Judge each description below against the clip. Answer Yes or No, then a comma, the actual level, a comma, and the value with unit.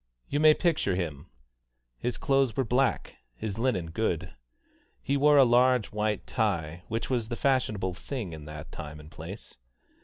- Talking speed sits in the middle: Yes, average, 160 wpm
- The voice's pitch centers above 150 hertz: No, low, 110 Hz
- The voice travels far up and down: Yes, wide, 7.1 semitones